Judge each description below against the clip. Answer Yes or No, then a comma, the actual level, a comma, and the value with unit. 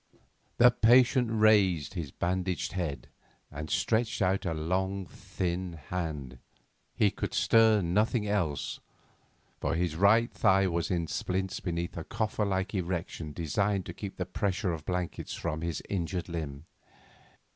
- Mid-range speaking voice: No, very low, 90 Hz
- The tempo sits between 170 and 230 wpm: No, average, 145 wpm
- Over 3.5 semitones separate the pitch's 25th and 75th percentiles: No, average, 3.2 semitones